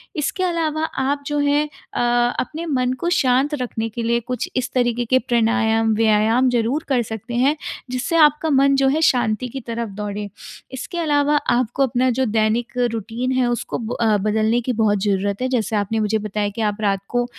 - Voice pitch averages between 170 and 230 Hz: No, high, 240 Hz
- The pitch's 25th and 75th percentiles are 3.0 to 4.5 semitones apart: Yes, average, 3.5 semitones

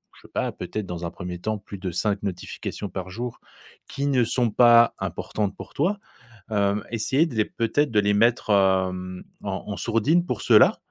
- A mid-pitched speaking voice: No, low, 105 Hz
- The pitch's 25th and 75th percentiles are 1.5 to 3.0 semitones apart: No, average, 3.7 semitones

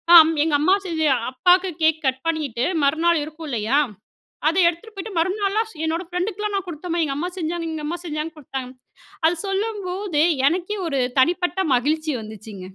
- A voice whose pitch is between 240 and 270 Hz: No, very high, 330 Hz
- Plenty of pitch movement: No, average, 3.3 semitones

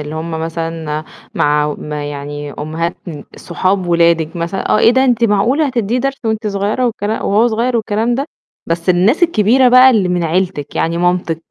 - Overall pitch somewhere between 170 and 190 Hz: Yes, medium, 185 Hz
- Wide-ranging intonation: Yes, wide, 5.9 semitones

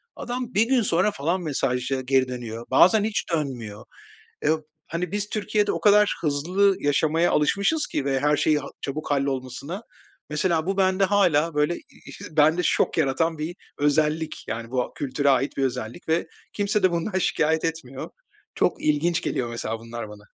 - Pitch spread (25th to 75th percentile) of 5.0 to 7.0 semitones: Yes, wide, 5.6 semitones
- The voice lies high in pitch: No, medium, 155 Hz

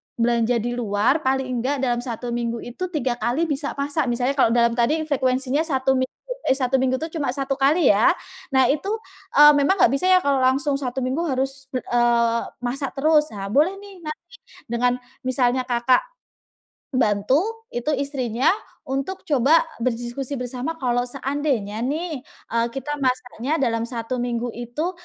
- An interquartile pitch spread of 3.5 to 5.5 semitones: No, average, 3.1 semitones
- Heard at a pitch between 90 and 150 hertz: No, very high, 260 Hz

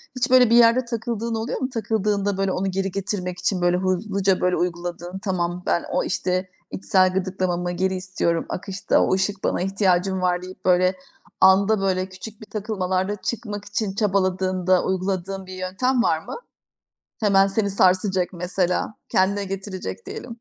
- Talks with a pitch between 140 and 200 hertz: Yes, high, 190 Hz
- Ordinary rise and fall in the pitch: No, narrow, 1.9 semitones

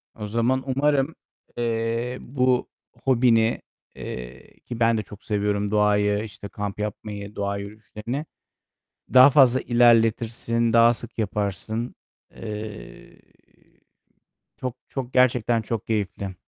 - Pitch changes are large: No, average, 2.8 semitones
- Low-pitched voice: Yes, low, 115 Hz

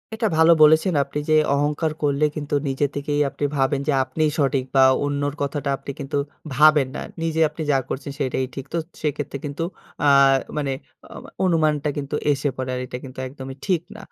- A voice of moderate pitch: Yes, medium, 145 Hz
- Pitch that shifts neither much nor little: No, narrow, 2.0 semitones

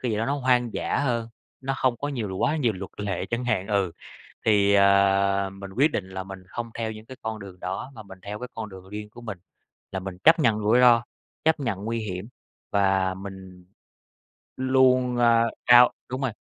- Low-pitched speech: Yes, low, 110 Hz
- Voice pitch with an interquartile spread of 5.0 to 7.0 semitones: No, average, 4.0 semitones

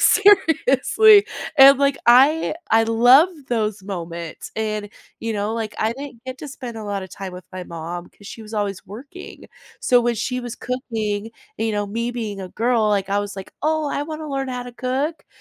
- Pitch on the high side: Yes, high, 230 Hz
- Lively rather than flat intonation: No, average, 4.7 semitones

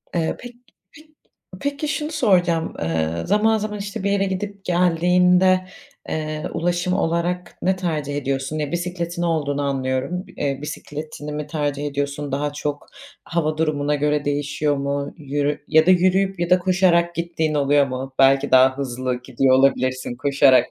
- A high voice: No, medium, 155 Hz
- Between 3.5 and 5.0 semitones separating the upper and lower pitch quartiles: Yes, average, 4.2 semitones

